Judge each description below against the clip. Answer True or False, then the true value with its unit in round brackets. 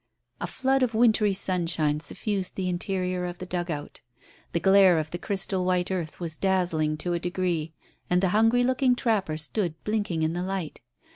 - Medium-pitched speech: True (180 Hz)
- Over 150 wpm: True (175 wpm)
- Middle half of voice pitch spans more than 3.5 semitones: False (3.0 semitones)